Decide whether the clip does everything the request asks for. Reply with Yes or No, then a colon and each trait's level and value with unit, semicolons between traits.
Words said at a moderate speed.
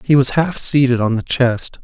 No: fast, 230 wpm